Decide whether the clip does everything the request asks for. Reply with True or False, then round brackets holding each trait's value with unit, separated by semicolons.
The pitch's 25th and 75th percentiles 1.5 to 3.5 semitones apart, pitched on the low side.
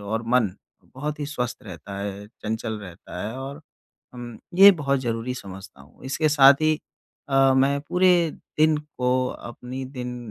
False (4.3 semitones; 125 Hz)